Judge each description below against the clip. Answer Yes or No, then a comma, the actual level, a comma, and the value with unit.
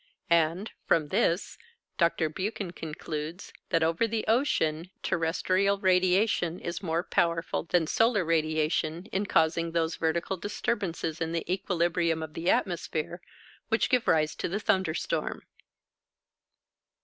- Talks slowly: Yes, slow, 125 wpm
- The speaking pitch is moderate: Yes, medium, 170 Hz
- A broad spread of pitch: No, average, 2.7 semitones